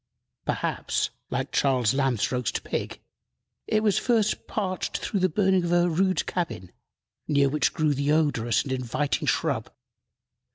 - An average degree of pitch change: No, wide, 6.0 semitones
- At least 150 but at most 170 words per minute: No, average, 140 wpm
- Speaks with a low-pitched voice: No, medium, 150 Hz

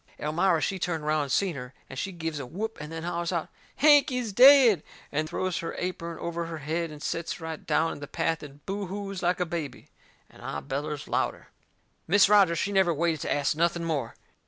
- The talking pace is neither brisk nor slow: No, fast, 215 wpm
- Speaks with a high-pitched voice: No, medium, 170 Hz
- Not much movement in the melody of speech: No, average, 3.7 semitones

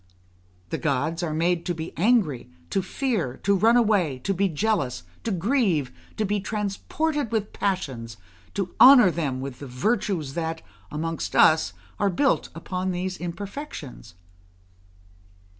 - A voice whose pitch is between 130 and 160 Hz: No, medium, 180 Hz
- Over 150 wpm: No, average, 140 wpm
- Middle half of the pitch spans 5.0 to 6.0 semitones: Yes, wide, 5.4 semitones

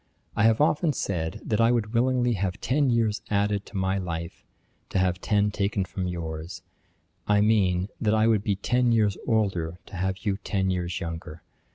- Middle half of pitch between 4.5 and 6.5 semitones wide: No, average, 3.5 semitones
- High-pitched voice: No, low, 100 Hz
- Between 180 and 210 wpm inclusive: Yes, average, 185 wpm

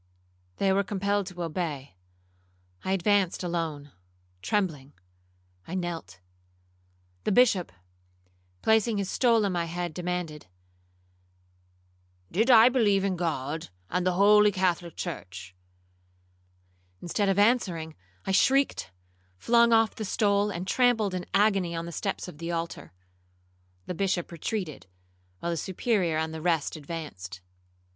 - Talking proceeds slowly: Yes, slow, 125 wpm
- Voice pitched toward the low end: No, medium, 180 Hz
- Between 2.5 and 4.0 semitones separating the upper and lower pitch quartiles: Yes, average, 3.7 semitones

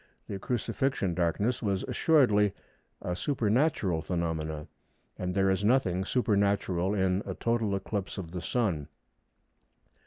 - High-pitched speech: No, low, 100 Hz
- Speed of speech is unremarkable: No, slow, 120 wpm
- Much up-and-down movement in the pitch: No, average, 3.8 semitones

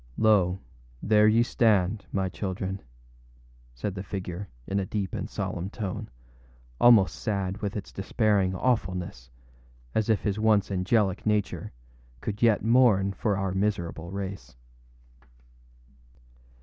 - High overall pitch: No, low, 100 Hz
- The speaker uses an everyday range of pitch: No, narrow, 2.3 semitones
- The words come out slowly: Yes, slow, 125 wpm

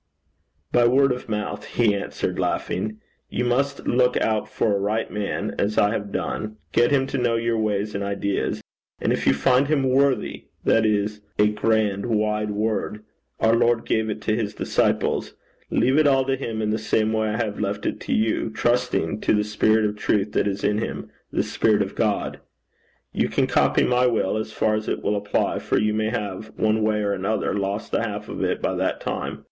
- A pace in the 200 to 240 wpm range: Yes, fast, 205 wpm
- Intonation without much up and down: Yes, narrow, 2.0 semitones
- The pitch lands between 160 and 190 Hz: No, low, 110 Hz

